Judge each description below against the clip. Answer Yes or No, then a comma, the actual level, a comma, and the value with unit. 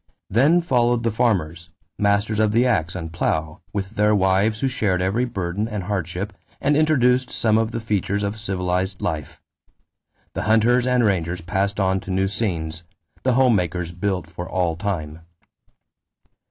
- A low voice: Yes, low, 100 Hz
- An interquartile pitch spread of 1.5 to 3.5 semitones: No, average, 4.0 semitones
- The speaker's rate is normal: Yes, average, 160 wpm